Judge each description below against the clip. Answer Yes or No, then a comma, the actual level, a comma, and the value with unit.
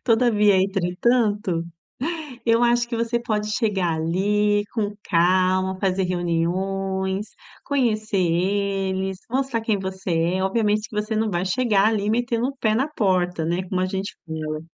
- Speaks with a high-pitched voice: Yes, high, 200 Hz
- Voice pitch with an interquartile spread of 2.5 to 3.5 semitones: Yes, average, 3.0 semitones